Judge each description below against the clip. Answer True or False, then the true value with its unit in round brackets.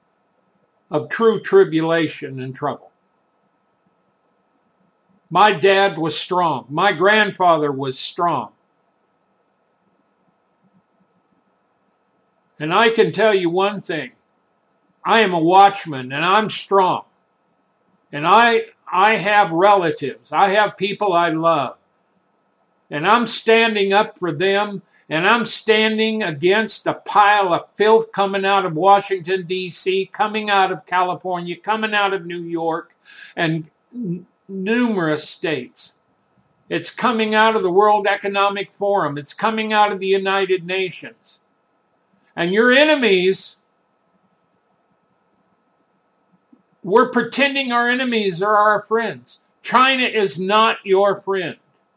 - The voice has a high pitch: True (195 Hz)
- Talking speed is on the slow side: True (115 wpm)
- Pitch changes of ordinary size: True (3.2 semitones)